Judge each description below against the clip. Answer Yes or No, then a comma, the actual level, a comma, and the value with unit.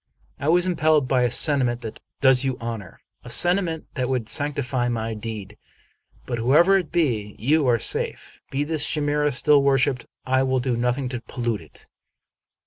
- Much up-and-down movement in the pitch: No, average, 3.8 semitones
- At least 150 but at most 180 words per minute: Yes, average, 175 wpm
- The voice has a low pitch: Yes, low, 130 Hz